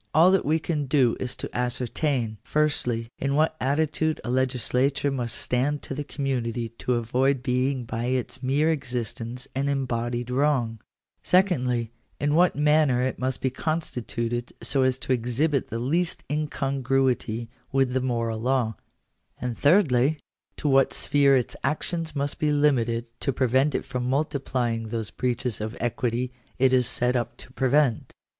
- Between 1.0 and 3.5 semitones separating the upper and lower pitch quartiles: Yes, average, 3.0 semitones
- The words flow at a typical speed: Yes, average, 160 wpm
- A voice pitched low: Yes, low, 130 Hz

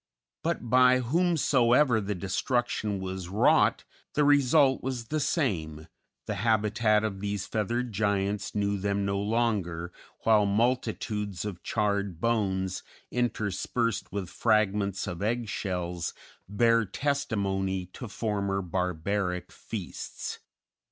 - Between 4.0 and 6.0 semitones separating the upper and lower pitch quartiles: No, average, 3.5 semitones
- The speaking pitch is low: Yes, low, 105 Hz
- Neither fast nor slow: No, slow, 110 wpm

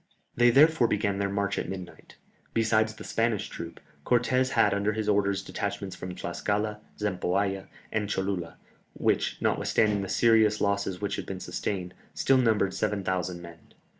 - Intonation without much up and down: Yes, narrow, 2.1 semitones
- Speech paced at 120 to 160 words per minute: Yes, average, 150 wpm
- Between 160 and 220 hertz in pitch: No, low, 100 Hz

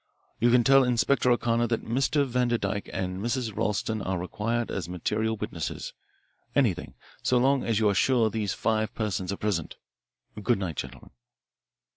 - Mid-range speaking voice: No, low, 110 Hz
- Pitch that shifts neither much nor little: Yes, average, 3.3 semitones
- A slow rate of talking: No, average, 160 wpm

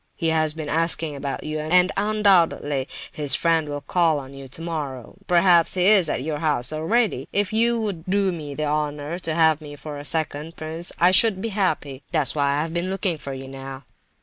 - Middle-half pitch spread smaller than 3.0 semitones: No, average, 3.6 semitones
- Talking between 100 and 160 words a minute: No, average, 200 wpm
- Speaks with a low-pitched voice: No, medium, 160 Hz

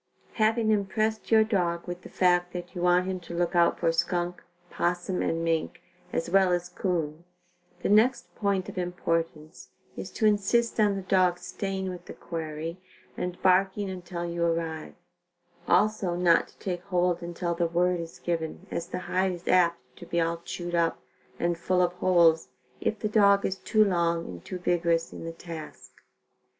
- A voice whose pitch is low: No, medium, 175 Hz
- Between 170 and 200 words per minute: Yes, average, 180 wpm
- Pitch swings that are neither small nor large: No, narrow, 2.0 semitones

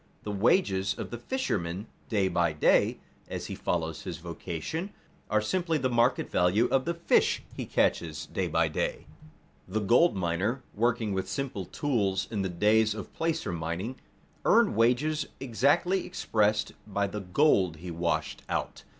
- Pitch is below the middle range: Yes, low, 105 Hz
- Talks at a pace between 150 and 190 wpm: Yes, average, 155 wpm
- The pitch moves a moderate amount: No, wide, 6.2 semitones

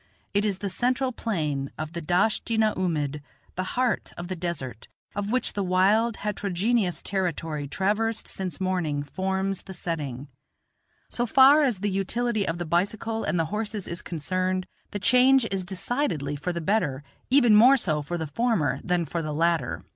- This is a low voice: No, high, 190 Hz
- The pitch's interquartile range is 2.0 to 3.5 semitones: No, average, 4.8 semitones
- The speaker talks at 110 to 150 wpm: No, average, 175 wpm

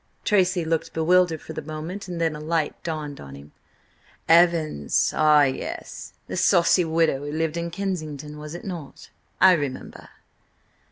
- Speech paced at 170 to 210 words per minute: No, average, 155 wpm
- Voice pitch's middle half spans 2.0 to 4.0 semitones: Yes, narrow, 2.4 semitones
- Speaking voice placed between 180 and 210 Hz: No, medium, 160 Hz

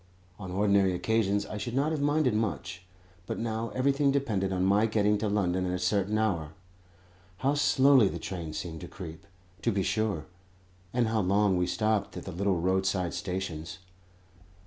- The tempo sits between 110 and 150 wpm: No, average, 170 wpm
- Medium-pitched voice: No, low, 100 Hz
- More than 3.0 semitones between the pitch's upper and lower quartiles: Yes, average, 3.4 semitones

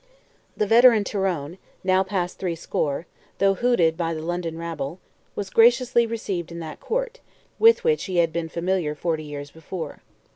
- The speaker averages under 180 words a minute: Yes, average, 155 wpm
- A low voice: No, medium, 180 Hz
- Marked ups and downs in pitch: No, average, 5.0 semitones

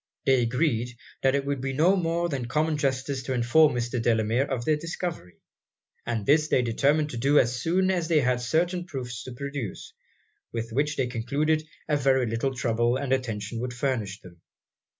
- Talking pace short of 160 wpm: No, average, 185 wpm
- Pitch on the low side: Yes, low, 130 Hz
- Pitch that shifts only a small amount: No, average, 4.1 semitones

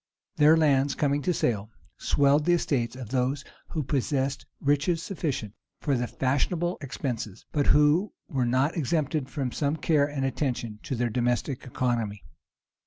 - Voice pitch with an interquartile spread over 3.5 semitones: No, average, 3.2 semitones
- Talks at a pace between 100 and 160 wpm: Yes, average, 150 wpm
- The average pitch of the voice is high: No, medium, 140 Hz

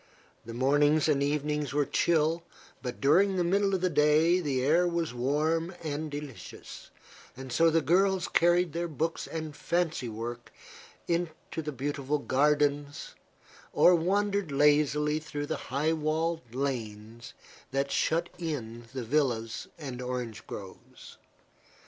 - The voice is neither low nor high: Yes, medium, 150 Hz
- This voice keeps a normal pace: No, slow, 130 wpm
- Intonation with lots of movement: No, average, 3.5 semitones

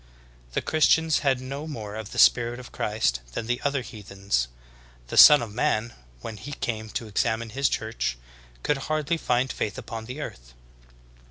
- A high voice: No, low, 115 Hz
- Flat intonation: No, average, 4.3 semitones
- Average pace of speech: Yes, average, 165 wpm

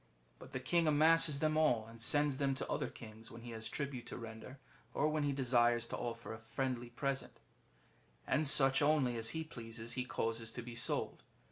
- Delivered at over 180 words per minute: Yes, average, 200 wpm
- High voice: No, low, 125 Hz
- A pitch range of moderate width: Yes, average, 4.0 semitones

